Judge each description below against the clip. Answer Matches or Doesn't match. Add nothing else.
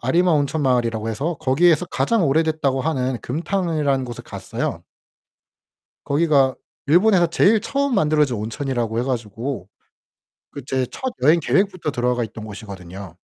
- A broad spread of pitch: Matches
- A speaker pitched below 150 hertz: Matches